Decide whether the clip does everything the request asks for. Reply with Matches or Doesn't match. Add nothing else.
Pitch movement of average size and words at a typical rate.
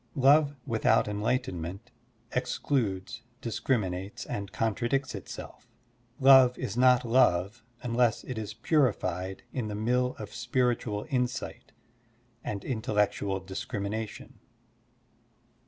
Doesn't match